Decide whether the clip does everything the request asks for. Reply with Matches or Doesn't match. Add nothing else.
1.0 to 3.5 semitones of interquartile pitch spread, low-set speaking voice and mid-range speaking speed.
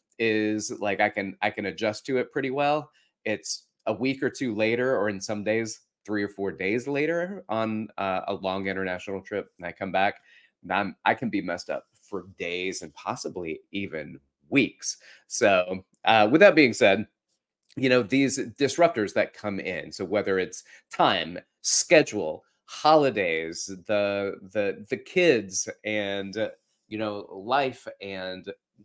Matches